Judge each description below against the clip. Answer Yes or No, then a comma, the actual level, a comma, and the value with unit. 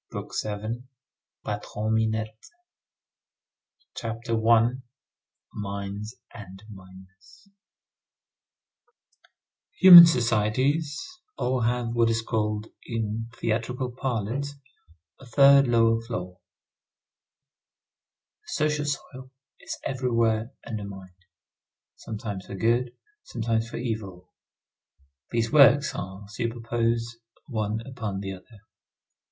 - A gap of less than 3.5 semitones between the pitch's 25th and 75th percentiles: Yes, average, 2.9 semitones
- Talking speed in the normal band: No, slow, 85 wpm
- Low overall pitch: Yes, low, 115 Hz